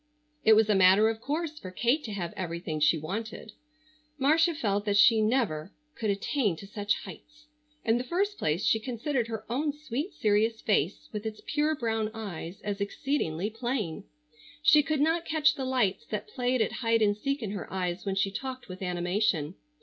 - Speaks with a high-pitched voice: Yes, high, 220 Hz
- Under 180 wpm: No, average, 190 wpm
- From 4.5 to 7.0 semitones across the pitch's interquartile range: Yes, wide, 5.4 semitones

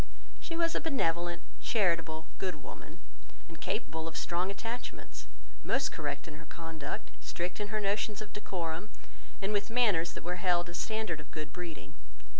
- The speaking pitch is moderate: Yes, medium, 175 Hz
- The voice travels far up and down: No, average, 4.3 semitones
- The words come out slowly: No, average, 165 wpm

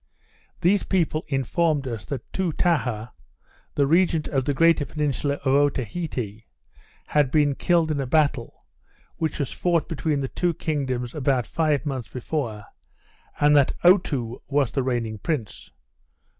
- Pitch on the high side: No, medium, 145 Hz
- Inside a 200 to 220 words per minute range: No, average, 140 wpm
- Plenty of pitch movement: No, average, 3.7 semitones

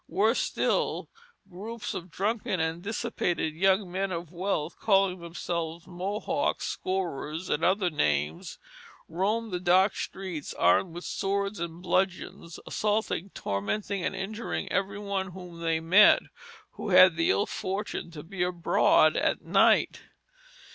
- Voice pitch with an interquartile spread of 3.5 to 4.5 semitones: No, average, 2.9 semitones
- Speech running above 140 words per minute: No, slow, 135 wpm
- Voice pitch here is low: No, medium, 185 Hz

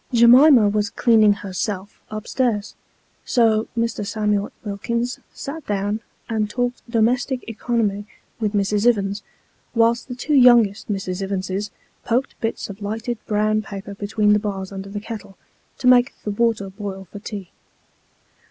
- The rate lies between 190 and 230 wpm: No, average, 150 wpm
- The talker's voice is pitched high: Yes, high, 215 Hz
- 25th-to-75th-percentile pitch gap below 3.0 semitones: Yes, narrow, 2.6 semitones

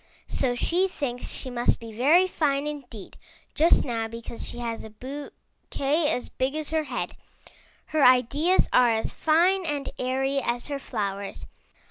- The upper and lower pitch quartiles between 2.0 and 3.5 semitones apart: No, average, 4.1 semitones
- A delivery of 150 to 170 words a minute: Yes, average, 155 wpm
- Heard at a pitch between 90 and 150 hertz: No, very high, 270 Hz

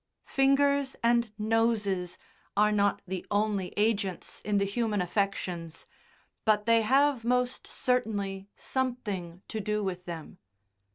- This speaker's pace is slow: Yes, slow, 120 wpm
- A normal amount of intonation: Yes, average, 3.4 semitones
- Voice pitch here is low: No, high, 210 Hz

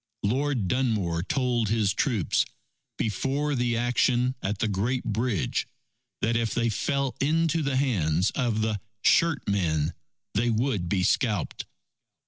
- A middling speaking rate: No, slow, 130 wpm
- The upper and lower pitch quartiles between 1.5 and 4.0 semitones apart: No, average, 4.4 semitones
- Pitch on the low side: Yes, low, 115 Hz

